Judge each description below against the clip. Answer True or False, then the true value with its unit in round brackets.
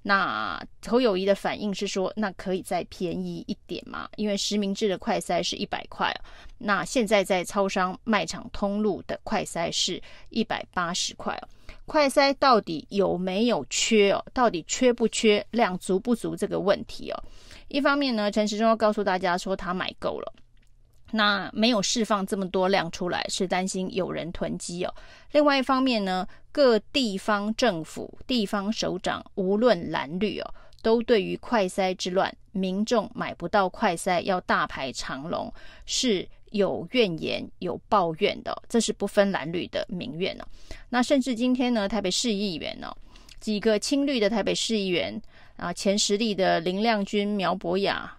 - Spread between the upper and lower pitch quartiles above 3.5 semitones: False (3.2 semitones)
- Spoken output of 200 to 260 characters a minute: True (250 characters per minute)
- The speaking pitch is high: True (205 Hz)